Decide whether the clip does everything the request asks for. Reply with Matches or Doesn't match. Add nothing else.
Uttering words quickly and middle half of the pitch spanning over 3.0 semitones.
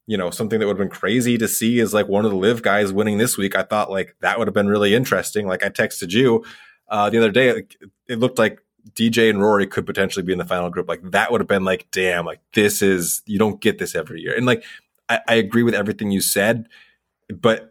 Doesn't match